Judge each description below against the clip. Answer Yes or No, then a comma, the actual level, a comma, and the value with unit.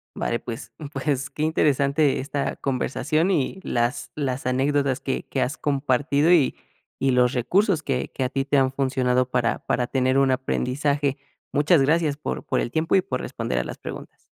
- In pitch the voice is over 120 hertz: Yes, low, 135 Hz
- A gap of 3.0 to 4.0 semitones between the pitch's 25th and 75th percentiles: No, narrow, 2.4 semitones